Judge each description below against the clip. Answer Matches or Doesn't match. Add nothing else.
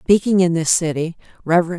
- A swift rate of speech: Doesn't match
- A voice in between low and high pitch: Matches